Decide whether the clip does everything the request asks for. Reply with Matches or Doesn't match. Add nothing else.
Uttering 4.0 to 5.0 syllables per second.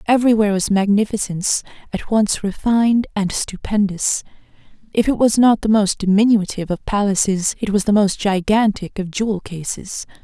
Doesn't match